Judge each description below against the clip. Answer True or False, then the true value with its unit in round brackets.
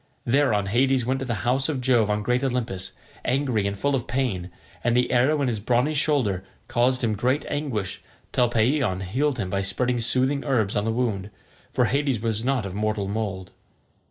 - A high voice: False (120 Hz)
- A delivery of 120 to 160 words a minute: False (190 wpm)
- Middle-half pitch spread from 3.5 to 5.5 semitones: True (4.0 semitones)